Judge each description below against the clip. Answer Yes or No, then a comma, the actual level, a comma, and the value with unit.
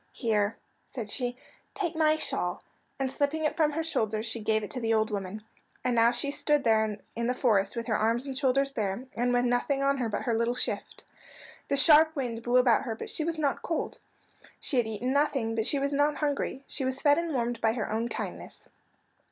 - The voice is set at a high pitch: Yes, high, 245 Hz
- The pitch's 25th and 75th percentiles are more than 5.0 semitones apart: No, average, 3.9 semitones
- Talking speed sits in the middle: No, fast, 220 wpm